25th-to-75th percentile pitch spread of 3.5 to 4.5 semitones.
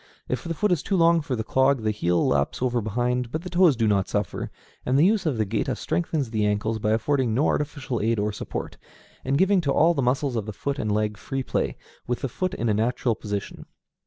No: average, 5.3 semitones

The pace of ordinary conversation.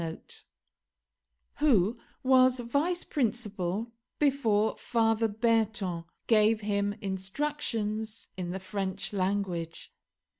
No: slow, 85 wpm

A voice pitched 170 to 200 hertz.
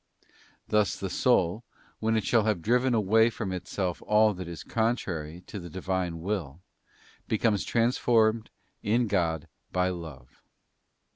No: low, 100 Hz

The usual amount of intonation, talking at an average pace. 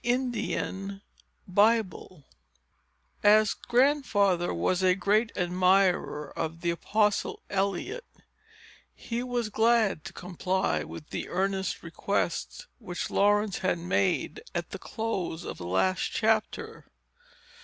No: average, 3.7 semitones; slow, 110 wpm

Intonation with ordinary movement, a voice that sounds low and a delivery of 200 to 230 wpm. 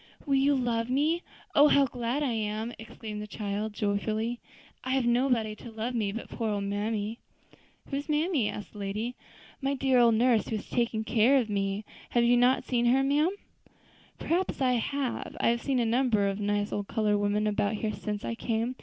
No: average, 3.4 semitones; high, 230 Hz; fast, 205 wpm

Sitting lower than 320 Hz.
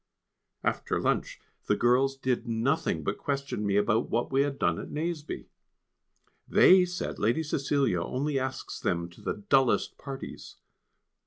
Yes: low, 135 Hz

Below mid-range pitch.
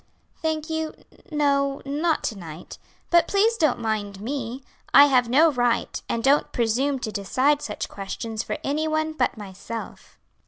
No: very high, 270 Hz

